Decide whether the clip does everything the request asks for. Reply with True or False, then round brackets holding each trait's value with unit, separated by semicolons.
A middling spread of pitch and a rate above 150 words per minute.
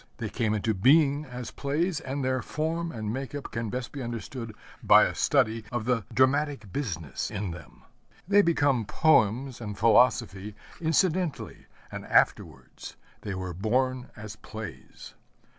False (5.0 semitones; 145 wpm)